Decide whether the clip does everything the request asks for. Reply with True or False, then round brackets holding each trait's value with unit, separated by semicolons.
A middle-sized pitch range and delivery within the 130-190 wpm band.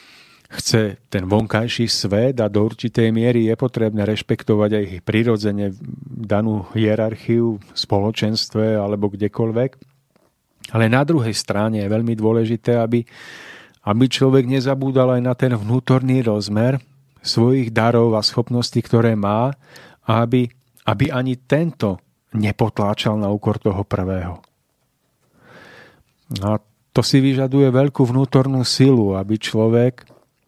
False (3.2 semitones; 120 wpm)